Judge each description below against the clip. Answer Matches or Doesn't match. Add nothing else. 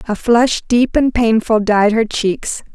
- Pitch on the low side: Doesn't match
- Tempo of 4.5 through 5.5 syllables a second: Doesn't match